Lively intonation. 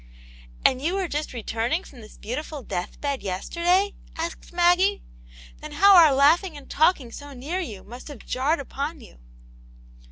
Yes: wide, 5.7 semitones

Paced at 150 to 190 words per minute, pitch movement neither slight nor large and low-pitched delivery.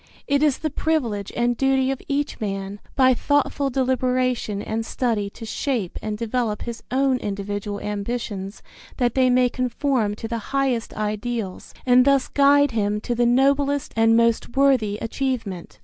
No: average, 155 wpm; average, 4.0 semitones; high, 240 Hz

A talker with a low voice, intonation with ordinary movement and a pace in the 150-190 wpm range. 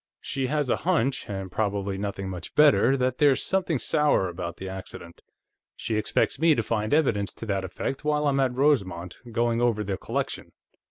No: low, 115 Hz; wide, 6.4 semitones; average, 180 wpm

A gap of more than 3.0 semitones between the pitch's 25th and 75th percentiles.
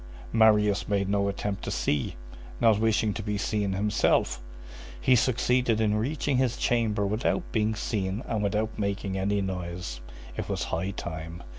No: narrow, 2.5 semitones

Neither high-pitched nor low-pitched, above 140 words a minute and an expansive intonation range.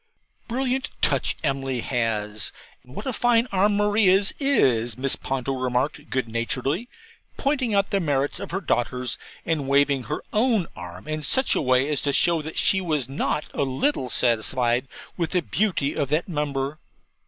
Yes: medium, 145 Hz; average, 165 wpm; wide, 7.3 semitones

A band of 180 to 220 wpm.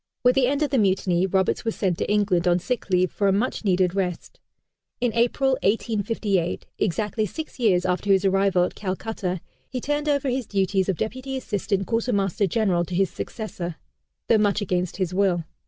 Yes: average, 185 wpm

